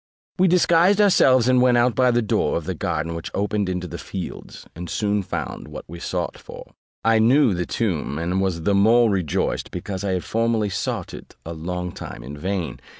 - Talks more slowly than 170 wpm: No, fast, 205 wpm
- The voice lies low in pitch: Yes, low, 100 Hz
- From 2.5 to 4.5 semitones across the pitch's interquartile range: No, average, 5.2 semitones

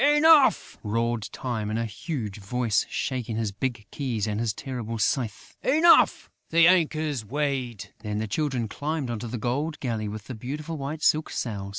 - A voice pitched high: No, low, 120 Hz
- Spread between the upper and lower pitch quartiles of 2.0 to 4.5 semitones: No, wide, 5.5 semitones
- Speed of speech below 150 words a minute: No, average, 170 wpm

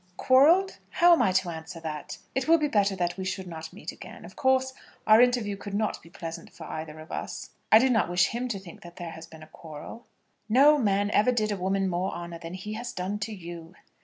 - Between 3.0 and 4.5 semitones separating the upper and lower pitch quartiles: No, wide, 5.6 semitones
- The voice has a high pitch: Yes, high, 195 Hz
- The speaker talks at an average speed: No, fast, 240 wpm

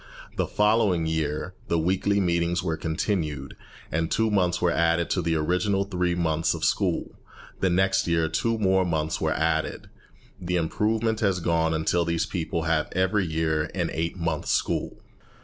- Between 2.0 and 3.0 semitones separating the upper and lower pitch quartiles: Yes, average, 2.7 semitones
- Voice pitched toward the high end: No, very low, 85 Hz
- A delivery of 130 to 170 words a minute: Yes, average, 165 wpm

